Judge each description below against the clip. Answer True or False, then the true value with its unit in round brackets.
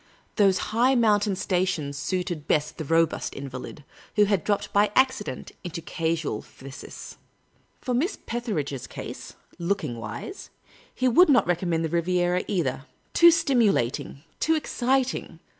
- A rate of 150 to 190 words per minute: False (140 wpm)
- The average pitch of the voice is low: False (185 Hz)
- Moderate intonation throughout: False (7.0 semitones)